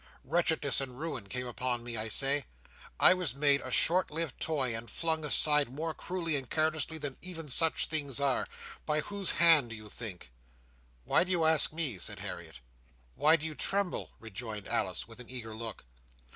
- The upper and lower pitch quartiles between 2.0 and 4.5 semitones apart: No, average, 4.9 semitones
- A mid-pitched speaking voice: Yes, medium, 145 Hz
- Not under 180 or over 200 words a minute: Yes, average, 185 wpm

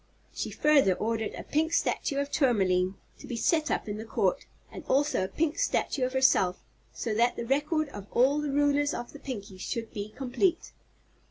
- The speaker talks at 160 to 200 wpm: Yes, average, 190 wpm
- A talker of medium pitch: No, very high, 260 Hz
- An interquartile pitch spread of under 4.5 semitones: No, wide, 5.4 semitones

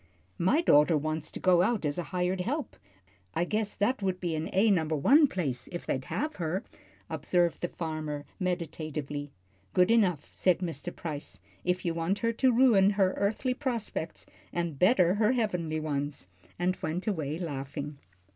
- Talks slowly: No, average, 165 wpm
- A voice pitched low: No, medium, 175 Hz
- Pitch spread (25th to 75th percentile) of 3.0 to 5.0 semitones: Yes, average, 4.6 semitones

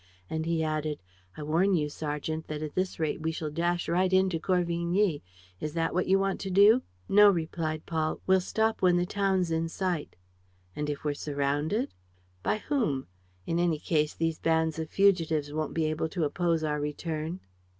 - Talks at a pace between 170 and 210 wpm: Yes, average, 180 wpm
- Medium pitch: Yes, medium, 165 Hz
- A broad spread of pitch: No, average, 3.1 semitones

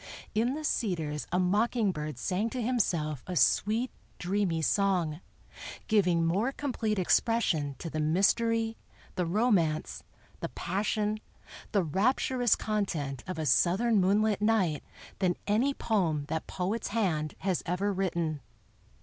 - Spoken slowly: Yes, slow, 130 wpm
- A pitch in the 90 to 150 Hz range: No, high, 190 Hz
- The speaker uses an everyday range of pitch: Yes, average, 4.9 semitones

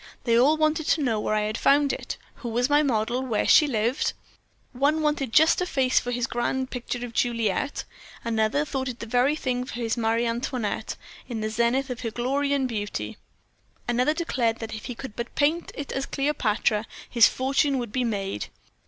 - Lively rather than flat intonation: No, average, 3.4 semitones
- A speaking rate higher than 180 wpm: Yes, average, 200 wpm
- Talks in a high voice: Yes, high, 245 Hz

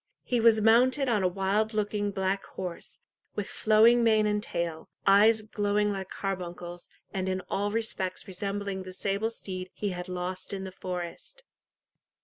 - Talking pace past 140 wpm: Yes, average, 155 wpm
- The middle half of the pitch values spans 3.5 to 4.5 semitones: No, narrow, 2.5 semitones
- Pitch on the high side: Yes, high, 200 Hz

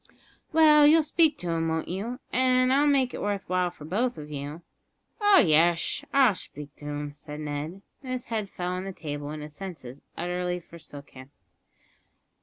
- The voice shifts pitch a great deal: Yes, wide, 9.0 semitones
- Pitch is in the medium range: Yes, medium, 180 Hz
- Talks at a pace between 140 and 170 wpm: No, average, 185 wpm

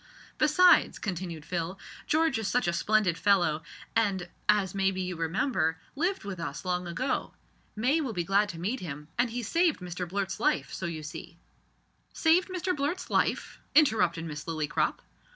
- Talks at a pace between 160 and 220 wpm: Yes, average, 170 wpm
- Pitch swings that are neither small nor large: No, wide, 6.7 semitones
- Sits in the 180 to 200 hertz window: Yes, high, 190 Hz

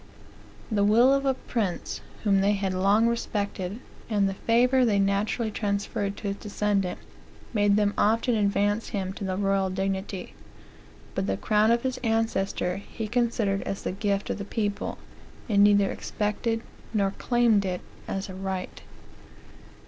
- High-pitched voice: Yes, high, 205 Hz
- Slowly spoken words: No, average, 155 wpm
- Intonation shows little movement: Yes, narrow, 2.3 semitones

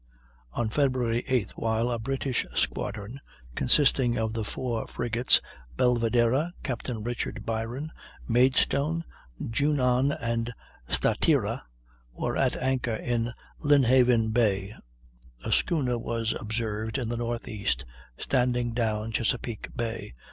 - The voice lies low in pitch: Yes, low, 120 Hz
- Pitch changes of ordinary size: No, narrow, 2.2 semitones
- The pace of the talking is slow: Yes, slow, 110 wpm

